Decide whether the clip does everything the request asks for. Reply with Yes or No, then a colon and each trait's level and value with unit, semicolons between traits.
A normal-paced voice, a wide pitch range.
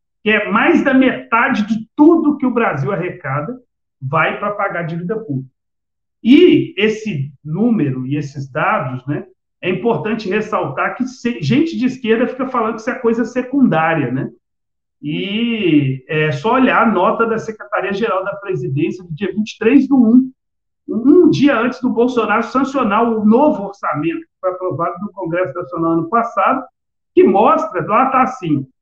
Yes: average, 160 wpm; wide, 6.6 semitones